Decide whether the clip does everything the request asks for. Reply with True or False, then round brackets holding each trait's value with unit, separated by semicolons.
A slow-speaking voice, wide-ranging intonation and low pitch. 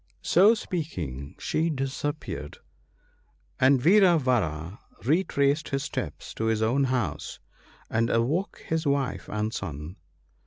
True (120 wpm; 6.4 semitones; 130 Hz)